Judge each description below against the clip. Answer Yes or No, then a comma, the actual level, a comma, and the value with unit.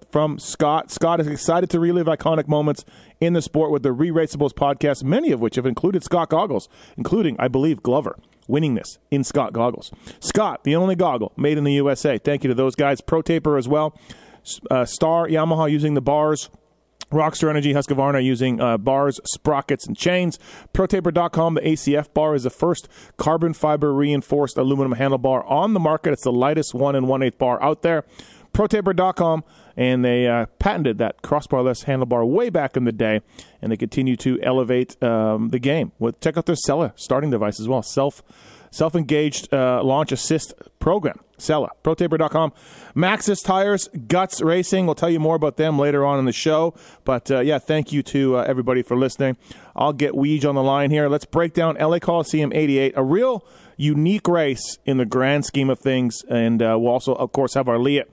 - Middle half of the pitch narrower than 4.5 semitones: Yes, average, 3.6 semitones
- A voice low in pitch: No, medium, 145 Hz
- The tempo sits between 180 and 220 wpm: Yes, average, 190 wpm